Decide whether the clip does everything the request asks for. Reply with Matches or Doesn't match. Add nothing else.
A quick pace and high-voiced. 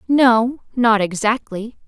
Doesn't match